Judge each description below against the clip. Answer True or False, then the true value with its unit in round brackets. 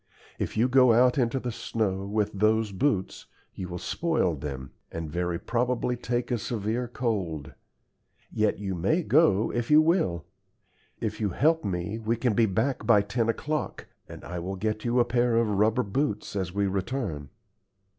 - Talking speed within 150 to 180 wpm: True (175 wpm)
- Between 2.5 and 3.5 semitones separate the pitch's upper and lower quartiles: False (4.4 semitones)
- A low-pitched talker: True (110 Hz)